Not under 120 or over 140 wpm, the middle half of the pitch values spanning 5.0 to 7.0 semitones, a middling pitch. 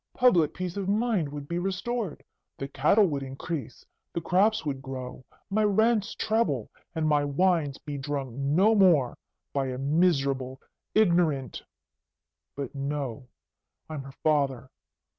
Yes: slow, 135 wpm; wide, 5.4 semitones; medium, 150 Hz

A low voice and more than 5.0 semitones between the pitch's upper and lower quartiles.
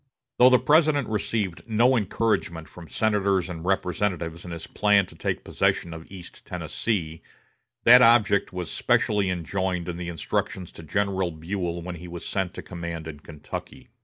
No: very low, 90 Hz; average, 3.6 semitones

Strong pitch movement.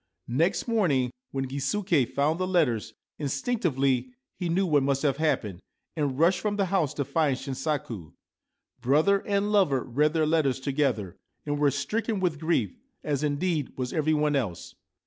No: average, 4.4 semitones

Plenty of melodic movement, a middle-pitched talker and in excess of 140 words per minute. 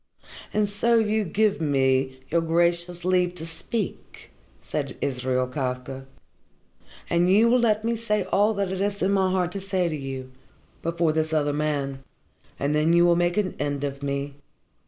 Yes: wide, 5.7 semitones; medium, 170 Hz; average, 170 wpm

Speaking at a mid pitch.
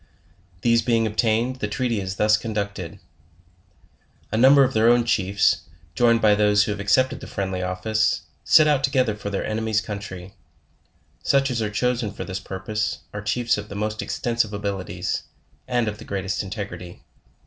No: low, 105 Hz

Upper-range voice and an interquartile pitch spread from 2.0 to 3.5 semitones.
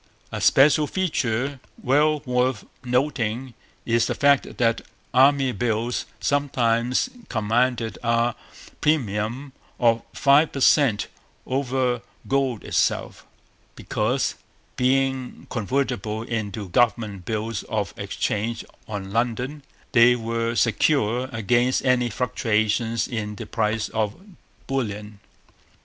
No: low, 120 Hz; average, 3.1 semitones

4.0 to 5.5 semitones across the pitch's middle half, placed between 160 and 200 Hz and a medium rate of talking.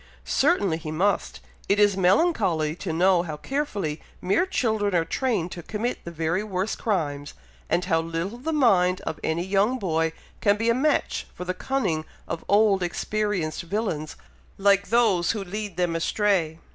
Yes: average, 4.4 semitones; high, 190 Hz; average, 165 wpm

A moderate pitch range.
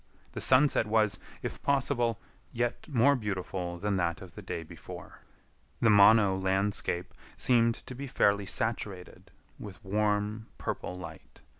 Yes: average, 3.6 semitones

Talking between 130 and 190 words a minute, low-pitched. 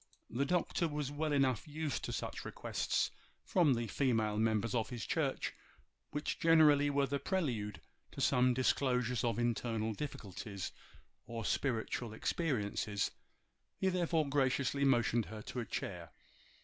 Yes: slow, 135 wpm; low, 125 Hz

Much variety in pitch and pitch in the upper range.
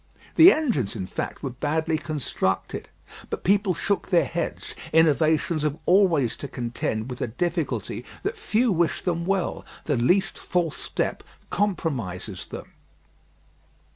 No: wide, 6.3 semitones; medium, 160 Hz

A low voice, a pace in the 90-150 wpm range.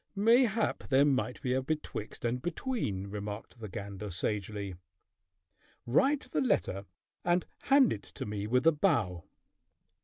Yes: low, 125 Hz; average, 140 wpm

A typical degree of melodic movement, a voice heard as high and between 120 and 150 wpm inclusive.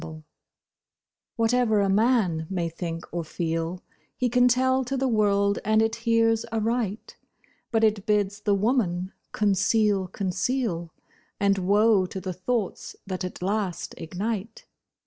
Yes: average, 3.6 semitones; high, 205 Hz; slow, 135 wpm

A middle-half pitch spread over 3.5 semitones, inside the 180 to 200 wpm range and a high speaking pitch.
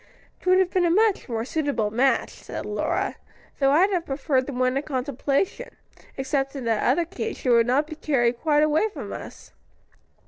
Yes: average, 4.6 semitones; average, 195 wpm; very high, 280 Hz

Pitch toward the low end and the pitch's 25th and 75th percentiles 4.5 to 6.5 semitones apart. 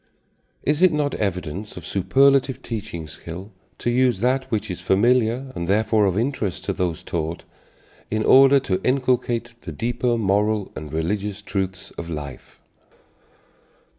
Yes: low, 110 Hz; average, 5.3 semitones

